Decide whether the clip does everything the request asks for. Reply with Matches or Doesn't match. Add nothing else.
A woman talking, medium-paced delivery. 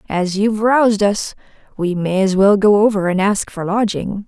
Matches